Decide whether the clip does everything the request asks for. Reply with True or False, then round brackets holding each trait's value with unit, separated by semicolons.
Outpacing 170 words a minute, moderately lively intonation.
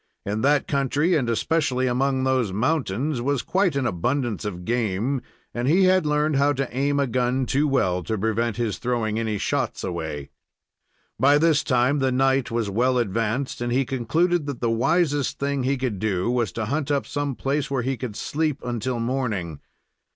True (185 wpm; 3.7 semitones)